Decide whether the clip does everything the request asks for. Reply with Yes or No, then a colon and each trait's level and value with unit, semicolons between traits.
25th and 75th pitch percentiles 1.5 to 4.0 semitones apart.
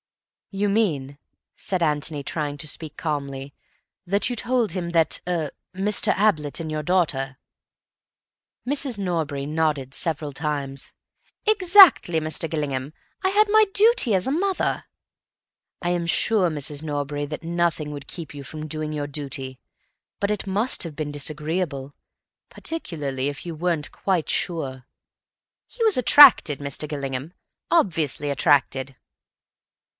No: average, 4.8 semitones